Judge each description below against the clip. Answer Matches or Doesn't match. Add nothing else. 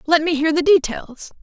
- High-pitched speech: Matches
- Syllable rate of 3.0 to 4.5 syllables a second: Doesn't match